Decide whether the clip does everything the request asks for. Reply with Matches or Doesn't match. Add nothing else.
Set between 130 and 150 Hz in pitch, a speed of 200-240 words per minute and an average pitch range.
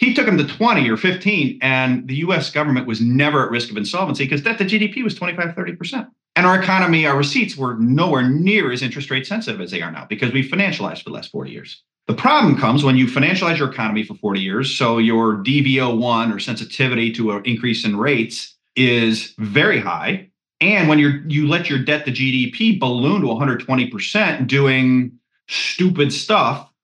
Doesn't match